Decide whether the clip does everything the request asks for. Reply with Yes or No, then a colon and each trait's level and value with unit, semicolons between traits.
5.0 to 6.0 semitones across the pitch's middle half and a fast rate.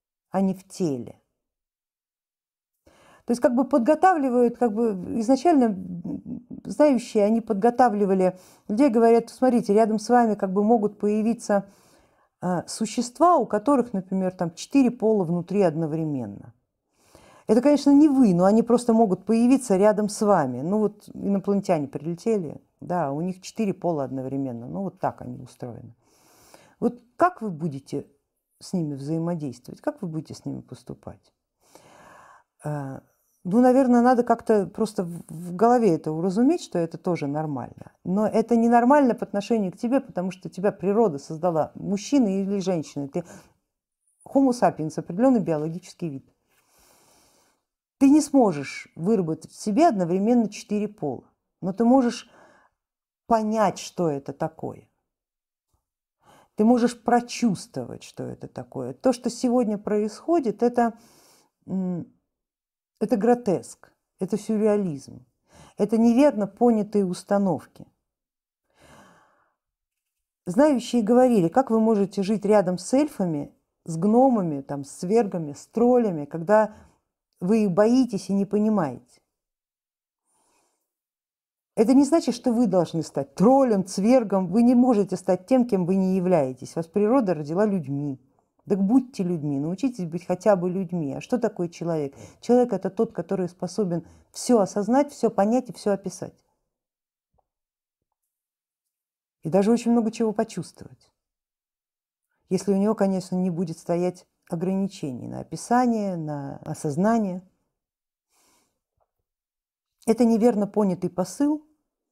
No: average, 5.3 semitones; average, 125 wpm